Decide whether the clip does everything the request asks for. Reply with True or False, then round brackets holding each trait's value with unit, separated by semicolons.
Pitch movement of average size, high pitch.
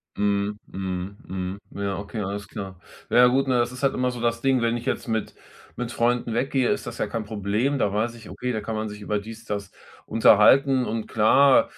False (3.2 semitones; 110 Hz)